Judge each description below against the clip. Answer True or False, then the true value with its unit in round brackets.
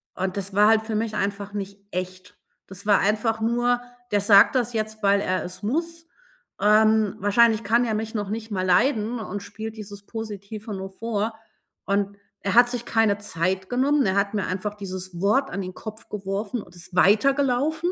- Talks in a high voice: True (210 Hz)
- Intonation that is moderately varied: False (2.3 semitones)